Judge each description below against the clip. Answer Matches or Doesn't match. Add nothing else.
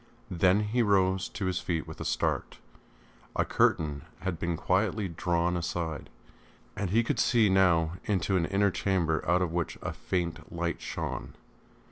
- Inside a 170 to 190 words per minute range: Doesn't match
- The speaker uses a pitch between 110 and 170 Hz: Doesn't match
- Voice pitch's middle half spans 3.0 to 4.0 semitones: Doesn't match